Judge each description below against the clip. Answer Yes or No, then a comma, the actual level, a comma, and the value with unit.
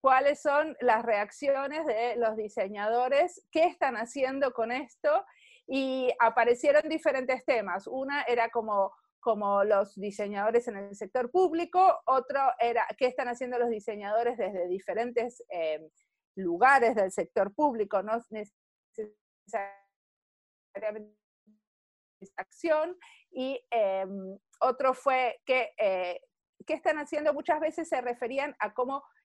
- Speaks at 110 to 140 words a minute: Yes, slow, 125 wpm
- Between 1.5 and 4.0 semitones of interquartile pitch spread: No, average, 5.3 semitones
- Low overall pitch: No, high, 245 Hz